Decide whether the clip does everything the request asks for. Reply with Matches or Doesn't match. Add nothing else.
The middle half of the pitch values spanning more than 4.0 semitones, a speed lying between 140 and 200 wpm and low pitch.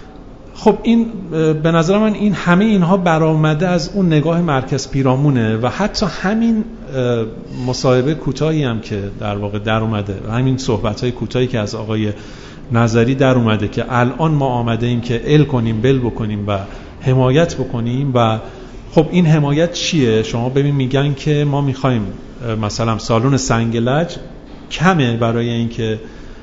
Matches